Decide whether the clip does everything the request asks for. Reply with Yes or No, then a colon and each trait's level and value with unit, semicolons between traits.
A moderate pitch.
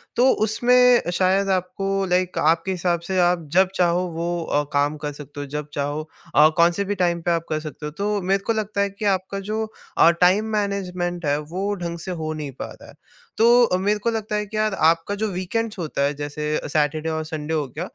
Yes: medium, 180 Hz